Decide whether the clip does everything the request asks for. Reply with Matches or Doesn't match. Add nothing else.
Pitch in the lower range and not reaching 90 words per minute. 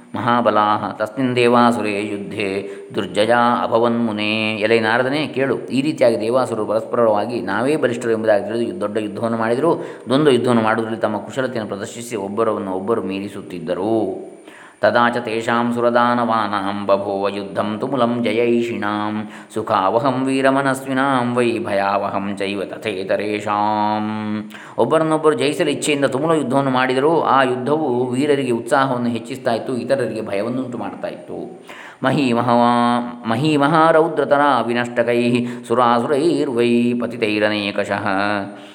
Doesn't match